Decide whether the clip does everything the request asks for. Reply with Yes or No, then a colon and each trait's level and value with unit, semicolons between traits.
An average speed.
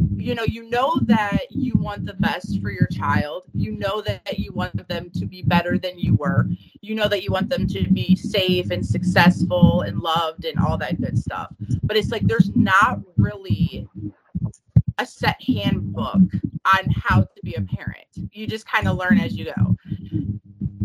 Yes: average, 185 wpm